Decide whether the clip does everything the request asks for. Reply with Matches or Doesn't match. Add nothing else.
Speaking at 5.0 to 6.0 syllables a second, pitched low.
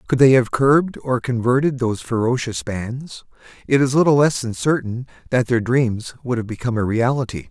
Matches